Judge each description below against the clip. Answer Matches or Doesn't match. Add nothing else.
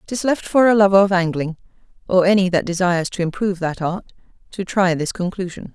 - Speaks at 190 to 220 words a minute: Matches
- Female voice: Matches